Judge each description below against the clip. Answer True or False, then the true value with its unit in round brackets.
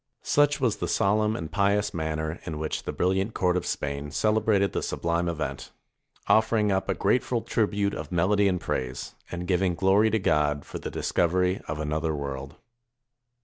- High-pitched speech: False (90 Hz)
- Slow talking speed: False (170 wpm)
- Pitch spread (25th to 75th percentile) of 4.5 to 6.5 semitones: True (4.8 semitones)